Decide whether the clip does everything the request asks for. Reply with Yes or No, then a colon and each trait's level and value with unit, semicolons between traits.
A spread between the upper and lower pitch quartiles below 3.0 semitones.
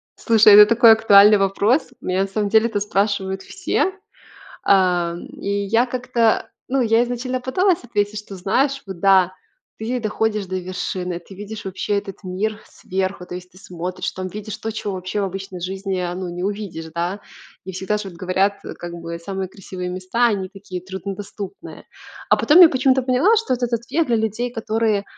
No: average, 3.3 semitones